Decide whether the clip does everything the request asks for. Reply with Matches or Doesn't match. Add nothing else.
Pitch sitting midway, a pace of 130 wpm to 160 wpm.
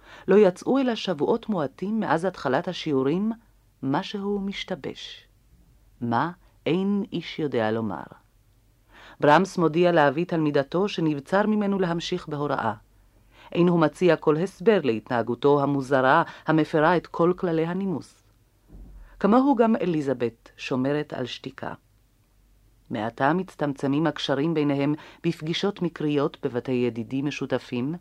Doesn't match